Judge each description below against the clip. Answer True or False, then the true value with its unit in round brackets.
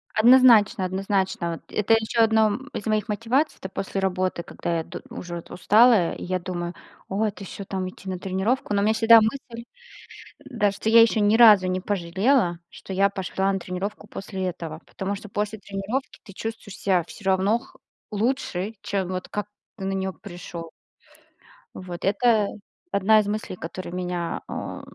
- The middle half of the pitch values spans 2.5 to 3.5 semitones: True (2.9 semitones)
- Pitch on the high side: True (200 Hz)